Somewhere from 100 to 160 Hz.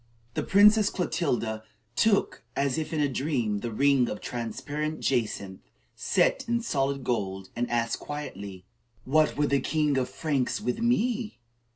Yes: medium, 140 Hz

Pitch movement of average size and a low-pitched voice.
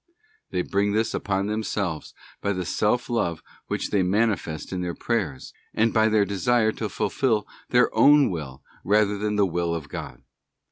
Yes: average, 3.4 semitones; low, 100 Hz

